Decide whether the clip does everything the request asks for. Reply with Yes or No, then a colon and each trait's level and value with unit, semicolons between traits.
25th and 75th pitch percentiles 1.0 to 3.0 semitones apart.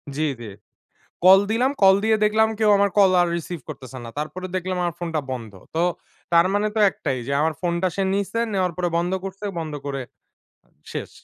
No: average, 4.1 semitones